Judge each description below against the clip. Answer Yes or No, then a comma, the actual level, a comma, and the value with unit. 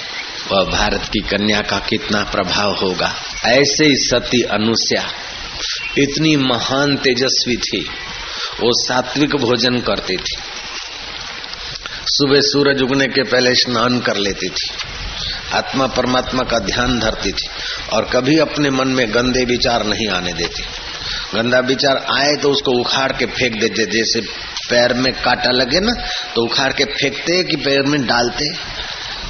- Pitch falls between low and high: No, low, 125 Hz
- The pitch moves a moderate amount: Yes, average, 3.5 semitones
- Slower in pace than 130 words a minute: No, average, 140 wpm